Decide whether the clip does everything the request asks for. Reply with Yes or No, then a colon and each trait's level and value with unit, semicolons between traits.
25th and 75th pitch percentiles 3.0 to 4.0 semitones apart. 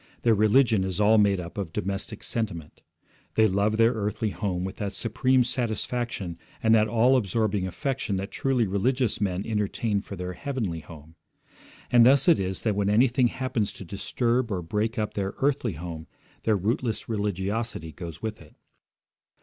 Yes: average, 3.5 semitones